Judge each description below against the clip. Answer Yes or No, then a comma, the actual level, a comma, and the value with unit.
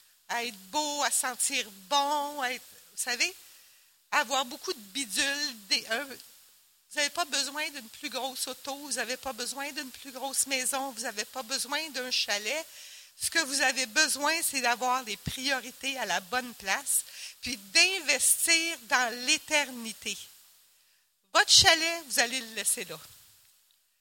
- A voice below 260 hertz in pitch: No, very high, 265 Hz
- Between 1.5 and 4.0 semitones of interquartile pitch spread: Yes, average, 3.4 semitones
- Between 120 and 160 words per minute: Yes, average, 155 wpm